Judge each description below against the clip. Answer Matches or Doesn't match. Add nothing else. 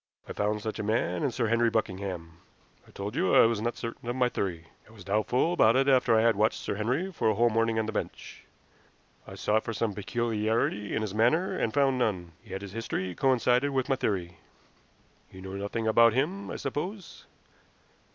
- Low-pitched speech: Matches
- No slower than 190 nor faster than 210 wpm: Matches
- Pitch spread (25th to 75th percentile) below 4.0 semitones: Matches